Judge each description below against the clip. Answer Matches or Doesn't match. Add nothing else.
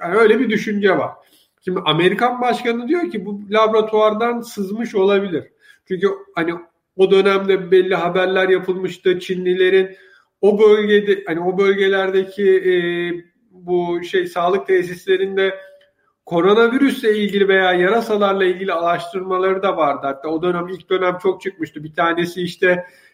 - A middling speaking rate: Matches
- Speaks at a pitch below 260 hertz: Matches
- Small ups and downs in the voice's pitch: Matches